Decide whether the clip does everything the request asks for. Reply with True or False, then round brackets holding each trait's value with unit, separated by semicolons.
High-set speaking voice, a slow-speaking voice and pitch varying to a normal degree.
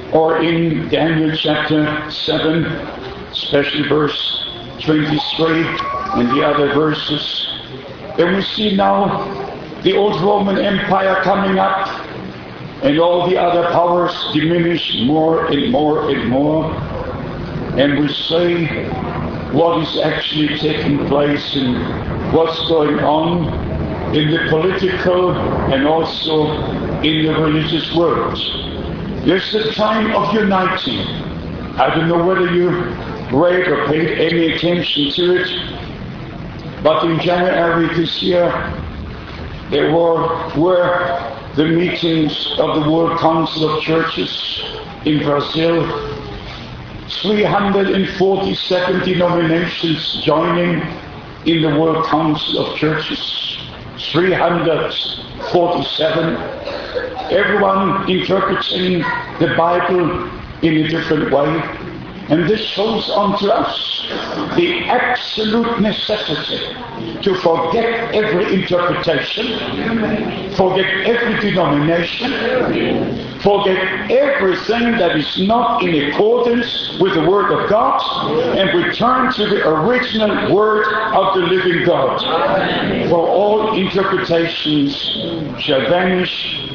False (170 Hz; 105 wpm; 3.7 semitones)